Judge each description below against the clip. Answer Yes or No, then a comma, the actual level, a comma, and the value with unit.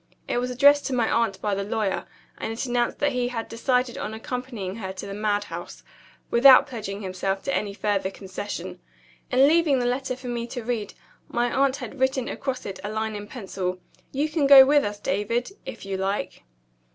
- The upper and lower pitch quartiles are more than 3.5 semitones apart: Yes, average, 4.2 semitones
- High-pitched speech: Yes, high, 235 Hz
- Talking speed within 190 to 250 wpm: Yes, average, 200 wpm